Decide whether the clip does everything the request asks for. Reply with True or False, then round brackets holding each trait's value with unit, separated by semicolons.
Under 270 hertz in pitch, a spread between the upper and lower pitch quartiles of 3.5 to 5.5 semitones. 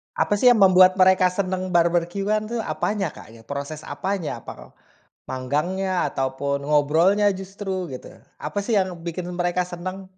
True (185 Hz; 3.8 semitones)